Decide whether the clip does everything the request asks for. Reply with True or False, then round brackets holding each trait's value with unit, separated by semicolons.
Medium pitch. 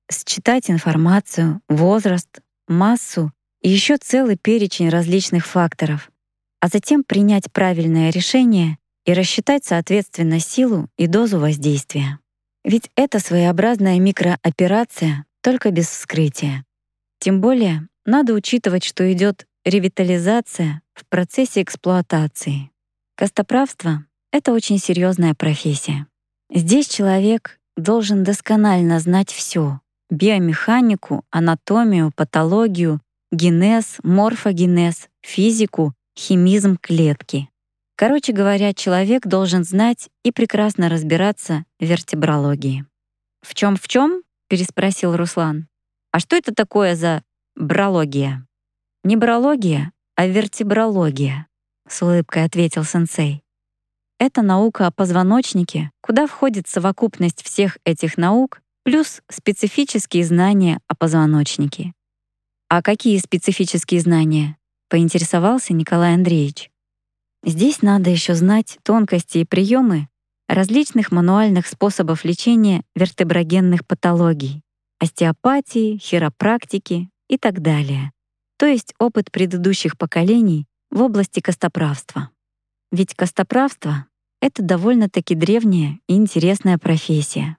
True (180 Hz)